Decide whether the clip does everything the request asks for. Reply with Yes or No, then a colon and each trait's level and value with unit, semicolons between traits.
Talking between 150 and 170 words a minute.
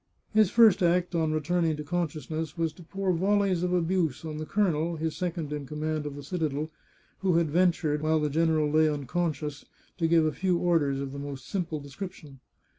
No: average, 195 wpm